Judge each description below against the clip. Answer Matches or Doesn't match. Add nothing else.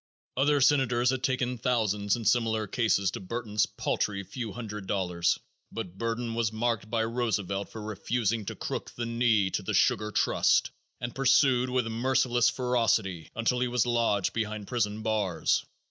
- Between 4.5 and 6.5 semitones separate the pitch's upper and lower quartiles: Doesn't match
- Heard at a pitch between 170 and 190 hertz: Doesn't match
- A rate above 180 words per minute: Doesn't match